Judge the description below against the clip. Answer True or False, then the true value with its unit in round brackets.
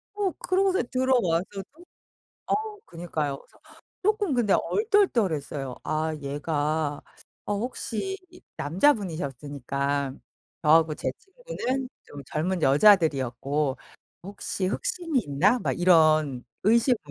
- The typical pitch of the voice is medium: True (175 Hz)